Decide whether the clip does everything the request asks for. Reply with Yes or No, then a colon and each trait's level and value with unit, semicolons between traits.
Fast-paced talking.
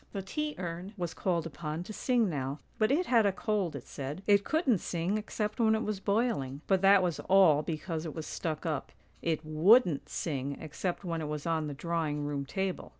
Yes: fast, 210 wpm